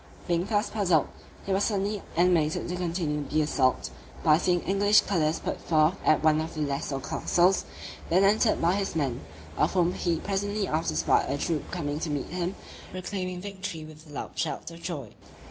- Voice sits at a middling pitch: Yes, medium, 170 Hz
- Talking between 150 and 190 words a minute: Yes, average, 180 wpm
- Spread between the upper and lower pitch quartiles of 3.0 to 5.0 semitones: Yes, average, 3.8 semitones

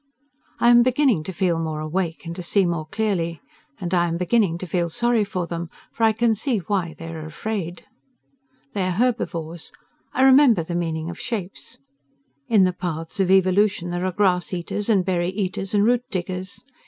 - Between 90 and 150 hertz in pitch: No, medium, 185 Hz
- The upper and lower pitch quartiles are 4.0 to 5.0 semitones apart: No, average, 3.6 semitones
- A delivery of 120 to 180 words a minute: No, average, 190 wpm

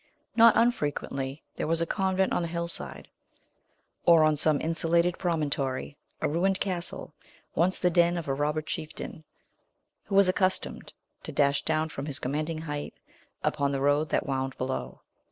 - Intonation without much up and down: No, average, 3.3 semitones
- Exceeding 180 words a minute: No, average, 155 wpm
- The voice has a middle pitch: Yes, medium, 160 Hz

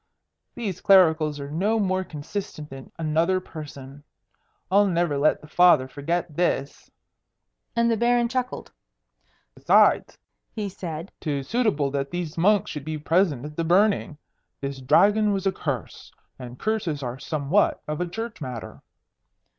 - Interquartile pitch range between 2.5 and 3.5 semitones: No, wide, 5.4 semitones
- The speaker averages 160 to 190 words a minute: No, average, 145 wpm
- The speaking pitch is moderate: Yes, medium, 165 Hz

